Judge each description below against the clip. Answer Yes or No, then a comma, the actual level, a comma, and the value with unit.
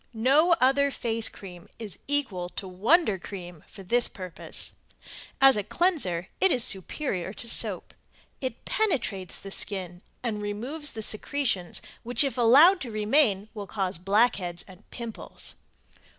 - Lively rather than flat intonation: Yes, wide, 6.2 semitones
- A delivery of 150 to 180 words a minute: No, average, 140 wpm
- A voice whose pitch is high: Yes, high, 215 Hz